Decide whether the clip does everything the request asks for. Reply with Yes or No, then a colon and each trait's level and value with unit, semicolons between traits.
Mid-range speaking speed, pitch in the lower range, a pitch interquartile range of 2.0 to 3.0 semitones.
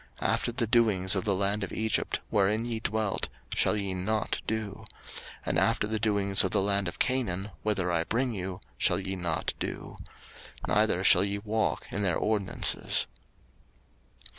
Yes: average, 165 wpm; low, 100 Hz; narrow, 2.4 semitones